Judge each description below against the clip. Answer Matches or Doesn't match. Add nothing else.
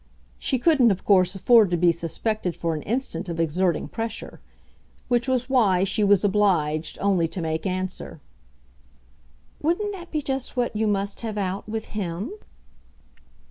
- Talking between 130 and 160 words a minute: Matches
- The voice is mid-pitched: Doesn't match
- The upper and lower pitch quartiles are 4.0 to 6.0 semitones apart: Matches